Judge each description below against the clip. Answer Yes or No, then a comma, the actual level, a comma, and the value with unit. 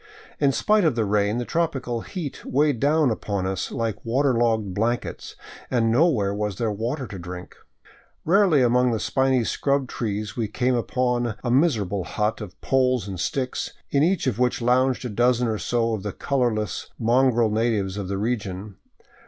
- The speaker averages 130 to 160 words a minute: No, average, 175 wpm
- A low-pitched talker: Yes, low, 120 Hz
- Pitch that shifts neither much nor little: Yes, average, 3.7 semitones